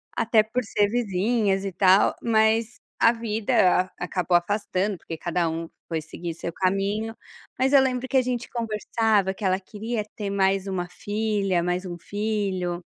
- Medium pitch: No, high, 205 Hz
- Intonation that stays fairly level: No, average, 3.3 semitones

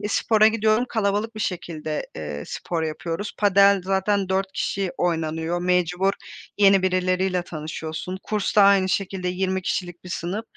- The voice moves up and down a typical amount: No, narrow, 2.3 semitones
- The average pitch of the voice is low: No, medium, 185 Hz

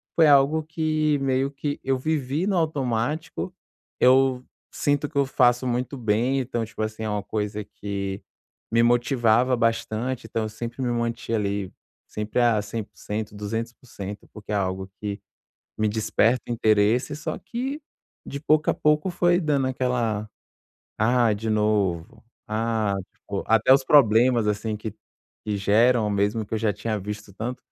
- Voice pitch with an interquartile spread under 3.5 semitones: No, average, 4.0 semitones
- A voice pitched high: No, low, 115 Hz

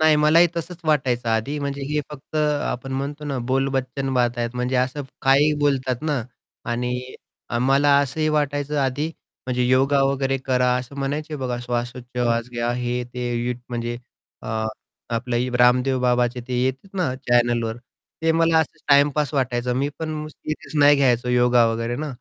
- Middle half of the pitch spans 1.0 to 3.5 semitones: Yes, average, 2.8 semitones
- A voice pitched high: No, low, 130 Hz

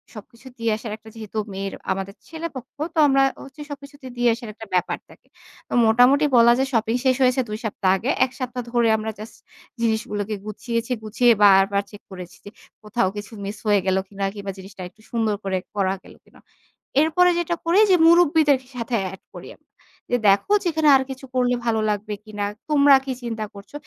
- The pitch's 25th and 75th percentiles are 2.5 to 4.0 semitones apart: No, average, 4.4 semitones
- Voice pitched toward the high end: Yes, high, 225 Hz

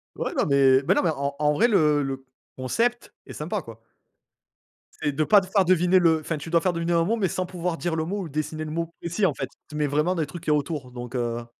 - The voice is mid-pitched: Yes, medium, 160 Hz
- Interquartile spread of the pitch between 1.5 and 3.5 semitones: No, average, 3.9 semitones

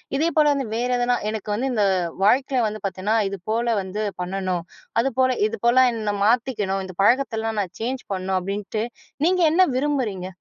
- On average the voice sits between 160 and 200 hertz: No, high, 225 Hz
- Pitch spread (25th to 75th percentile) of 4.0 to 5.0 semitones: Yes, average, 4.7 semitones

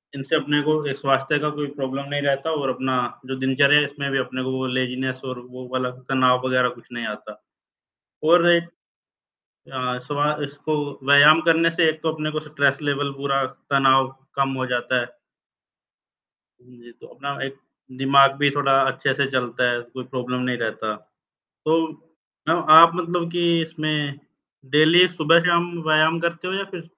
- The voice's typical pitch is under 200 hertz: Yes, medium, 140 Hz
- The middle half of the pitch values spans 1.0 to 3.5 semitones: Yes, average, 3.1 semitones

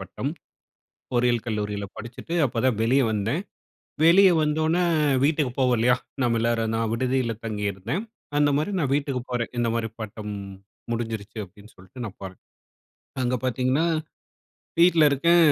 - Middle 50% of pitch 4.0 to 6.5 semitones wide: Yes, average, 4.3 semitones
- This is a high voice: No, low, 120 Hz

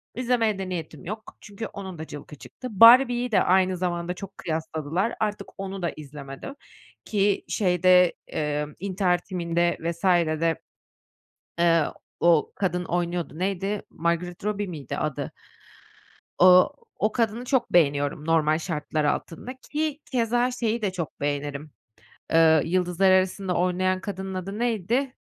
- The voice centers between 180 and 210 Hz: Yes, medium, 185 Hz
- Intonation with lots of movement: No, average, 3.9 semitones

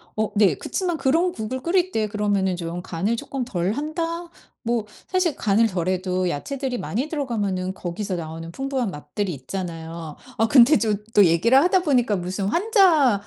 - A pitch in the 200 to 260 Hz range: Yes, high, 215 Hz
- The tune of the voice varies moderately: No, wide, 7.1 semitones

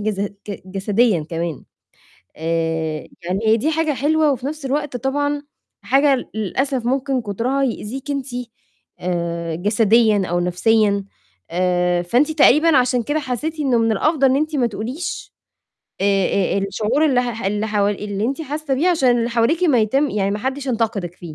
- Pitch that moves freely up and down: Yes, wide, 5.7 semitones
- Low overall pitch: No, high, 235 Hz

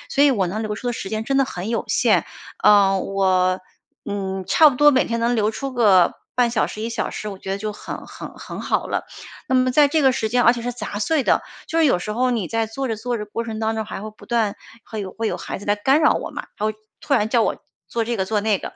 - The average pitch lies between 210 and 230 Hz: Yes, high, 220 Hz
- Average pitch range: Yes, average, 3.3 semitones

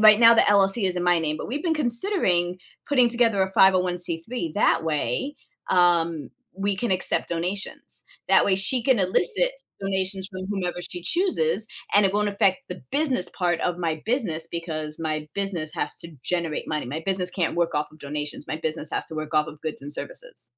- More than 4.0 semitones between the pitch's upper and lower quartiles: Yes, average, 4.5 semitones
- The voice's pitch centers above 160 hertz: Yes, medium, 185 Hz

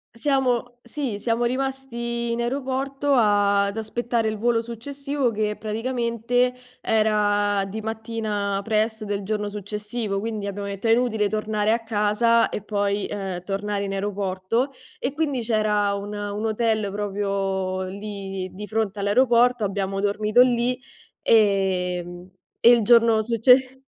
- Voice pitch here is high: Yes, high, 215 Hz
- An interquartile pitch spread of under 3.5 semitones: Yes, average, 2.8 semitones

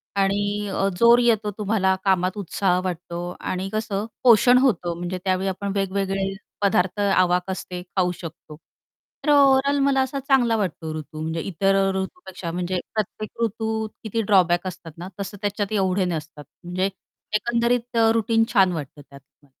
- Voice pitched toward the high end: Yes, high, 195 Hz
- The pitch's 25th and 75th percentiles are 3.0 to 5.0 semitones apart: Yes, average, 3.6 semitones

